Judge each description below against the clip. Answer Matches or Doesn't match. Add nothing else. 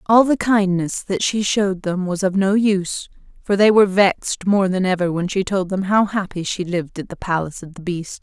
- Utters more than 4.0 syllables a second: Matches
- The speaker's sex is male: Doesn't match